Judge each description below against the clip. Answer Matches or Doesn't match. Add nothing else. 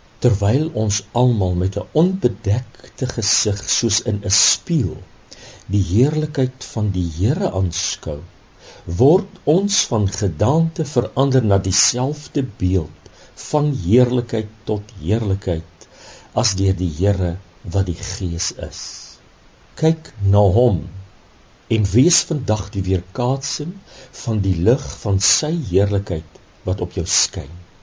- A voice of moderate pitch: Doesn't match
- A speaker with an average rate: Doesn't match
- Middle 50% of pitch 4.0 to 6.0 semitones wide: Matches